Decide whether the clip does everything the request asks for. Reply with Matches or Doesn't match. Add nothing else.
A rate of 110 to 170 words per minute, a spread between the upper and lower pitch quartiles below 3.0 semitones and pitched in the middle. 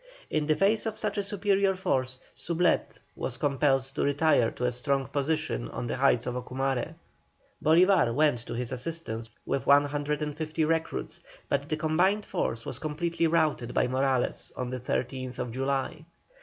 Doesn't match